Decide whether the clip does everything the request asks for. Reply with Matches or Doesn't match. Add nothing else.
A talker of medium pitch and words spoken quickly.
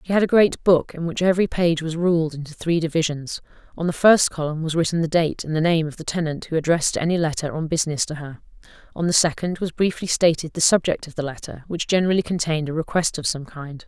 Matches